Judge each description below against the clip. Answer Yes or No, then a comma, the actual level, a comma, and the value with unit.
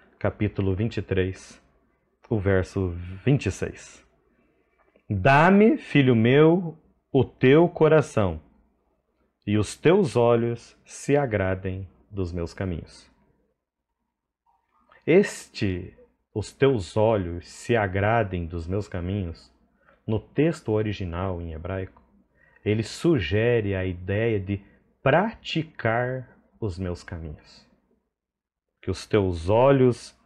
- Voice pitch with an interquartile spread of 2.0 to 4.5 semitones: No, average, 5.1 semitones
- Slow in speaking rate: Yes, slow, 95 wpm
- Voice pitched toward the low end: Yes, low, 105 Hz